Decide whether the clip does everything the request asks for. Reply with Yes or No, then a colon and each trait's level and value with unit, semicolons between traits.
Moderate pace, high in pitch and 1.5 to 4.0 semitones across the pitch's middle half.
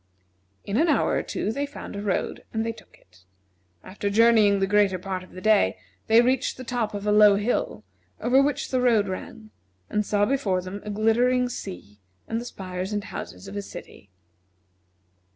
Yes: average, 190 wpm; high, 210 Hz; average, 3.2 semitones